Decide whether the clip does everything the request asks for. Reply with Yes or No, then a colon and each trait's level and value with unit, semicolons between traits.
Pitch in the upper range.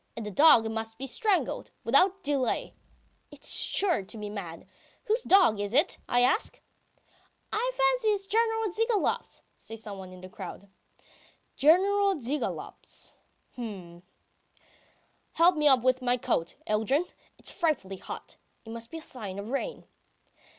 Yes: very high, 260 Hz